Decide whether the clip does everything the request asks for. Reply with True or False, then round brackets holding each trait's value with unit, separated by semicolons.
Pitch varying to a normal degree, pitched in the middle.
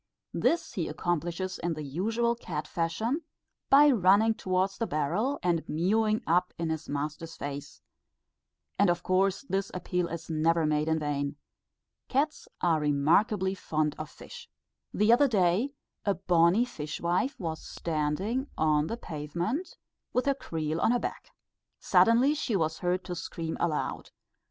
False (5.8 semitones; 175 Hz)